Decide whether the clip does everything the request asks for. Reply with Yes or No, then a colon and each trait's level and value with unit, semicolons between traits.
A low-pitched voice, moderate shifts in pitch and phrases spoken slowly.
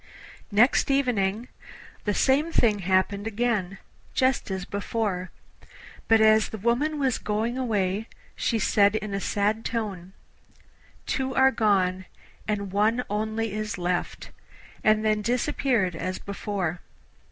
No: high, 215 Hz; average, 3.0 semitones; slow, 125 wpm